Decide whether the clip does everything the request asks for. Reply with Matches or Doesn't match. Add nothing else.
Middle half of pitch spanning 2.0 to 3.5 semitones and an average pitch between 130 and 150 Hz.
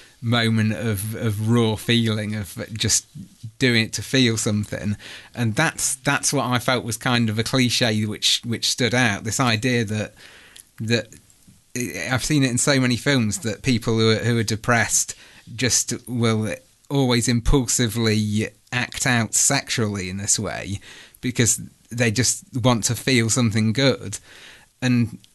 Doesn't match